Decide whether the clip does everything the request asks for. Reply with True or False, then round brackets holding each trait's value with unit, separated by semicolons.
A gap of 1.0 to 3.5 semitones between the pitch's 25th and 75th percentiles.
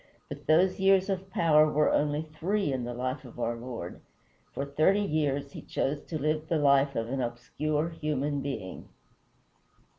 True (2.9 semitones)